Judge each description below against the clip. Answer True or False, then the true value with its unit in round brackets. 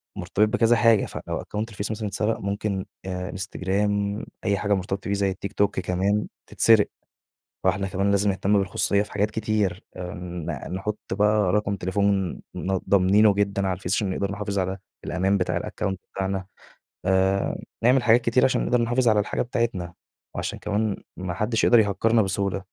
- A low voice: True (100 Hz)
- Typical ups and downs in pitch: False (1.9 semitones)